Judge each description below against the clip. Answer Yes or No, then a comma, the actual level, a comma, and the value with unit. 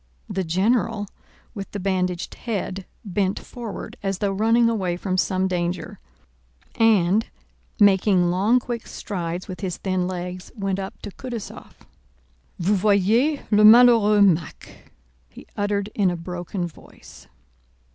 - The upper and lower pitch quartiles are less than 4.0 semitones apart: Yes, average, 2.7 semitones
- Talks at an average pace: No, slow, 130 wpm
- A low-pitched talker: No, high, 195 Hz